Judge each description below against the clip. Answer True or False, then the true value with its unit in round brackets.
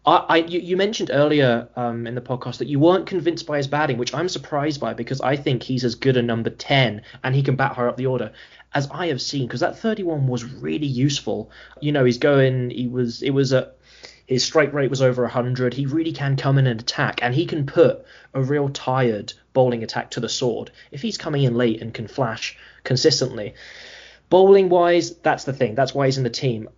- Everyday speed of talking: False (230 wpm)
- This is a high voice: False (135 Hz)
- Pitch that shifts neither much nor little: True (3.4 semitones)